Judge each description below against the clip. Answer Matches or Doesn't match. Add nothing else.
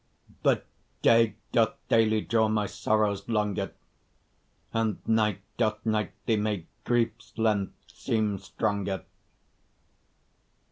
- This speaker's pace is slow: Matches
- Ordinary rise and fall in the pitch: Doesn't match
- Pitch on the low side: Matches